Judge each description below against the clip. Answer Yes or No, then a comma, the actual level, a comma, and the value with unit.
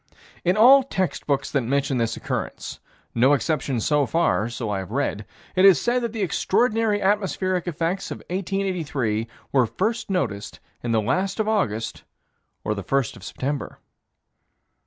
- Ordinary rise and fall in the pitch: No, wide, 8.7 semitones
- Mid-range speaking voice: Yes, medium, 155 Hz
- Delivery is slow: No, average, 155 wpm